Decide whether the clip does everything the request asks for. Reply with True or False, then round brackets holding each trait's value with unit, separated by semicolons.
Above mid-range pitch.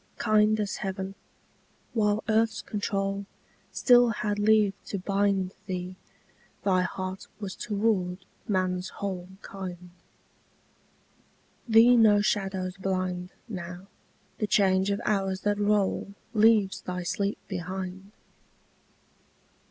True (195 Hz)